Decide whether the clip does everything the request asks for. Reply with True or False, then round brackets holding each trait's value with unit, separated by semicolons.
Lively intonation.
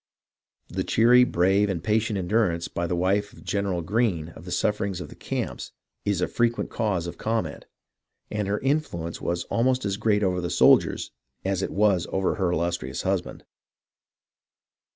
False (3.7 semitones)